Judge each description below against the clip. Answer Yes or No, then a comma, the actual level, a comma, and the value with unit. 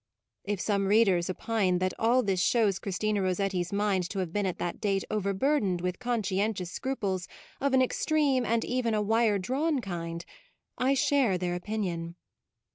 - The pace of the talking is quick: No, average, 165 wpm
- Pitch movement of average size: Yes, average, 4.1 semitones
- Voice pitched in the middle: No, high, 200 Hz